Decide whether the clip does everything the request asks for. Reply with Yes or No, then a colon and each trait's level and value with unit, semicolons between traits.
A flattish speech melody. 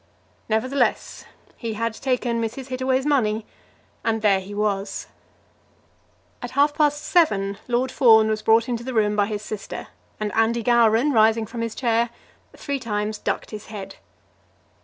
No: average, 3.0 semitones